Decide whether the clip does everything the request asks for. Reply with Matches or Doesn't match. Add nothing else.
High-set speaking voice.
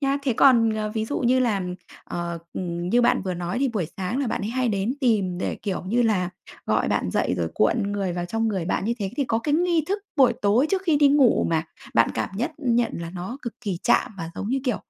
Matches